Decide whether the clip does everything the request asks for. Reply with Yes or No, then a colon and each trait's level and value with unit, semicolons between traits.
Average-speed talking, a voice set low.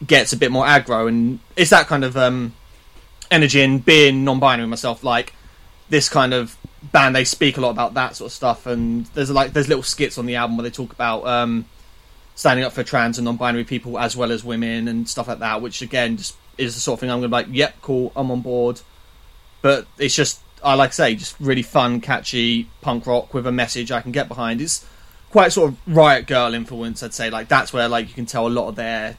No: fast, 240 wpm; low, 120 Hz